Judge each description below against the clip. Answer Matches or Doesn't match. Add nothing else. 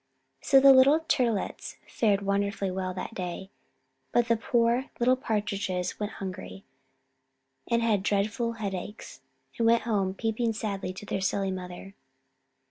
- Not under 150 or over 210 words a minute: Doesn't match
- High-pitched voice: Matches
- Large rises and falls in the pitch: Doesn't match